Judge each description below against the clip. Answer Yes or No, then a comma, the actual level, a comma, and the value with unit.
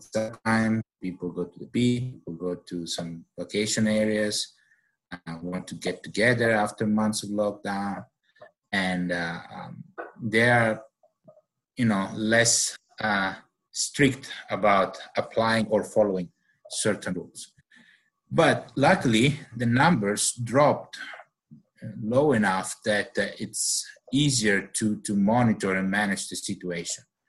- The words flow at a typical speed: No, slow, 125 wpm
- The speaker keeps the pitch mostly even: No, average, 3.5 semitones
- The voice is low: Yes, low, 110 Hz